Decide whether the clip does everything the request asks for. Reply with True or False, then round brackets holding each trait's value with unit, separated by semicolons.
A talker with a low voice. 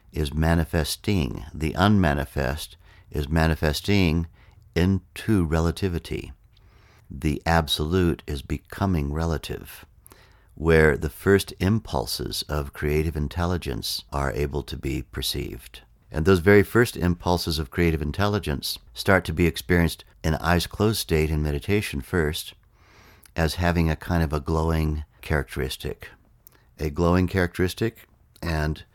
True (85 Hz)